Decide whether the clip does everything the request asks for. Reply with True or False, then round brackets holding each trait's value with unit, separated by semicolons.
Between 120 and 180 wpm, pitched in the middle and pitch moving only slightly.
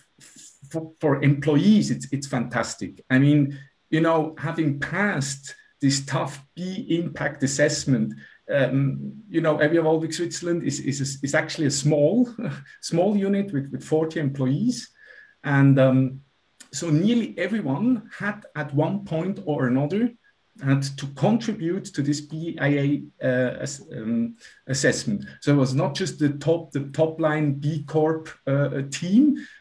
False (135 wpm; 155 Hz; 4.7 semitones)